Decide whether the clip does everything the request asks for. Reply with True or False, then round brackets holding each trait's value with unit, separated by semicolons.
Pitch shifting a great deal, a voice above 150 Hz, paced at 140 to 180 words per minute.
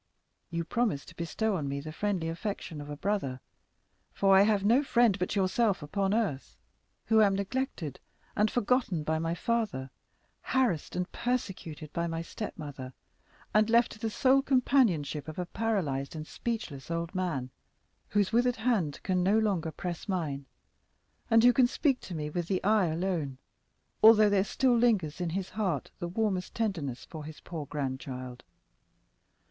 True (6.0 semitones; 185 Hz; 165 wpm)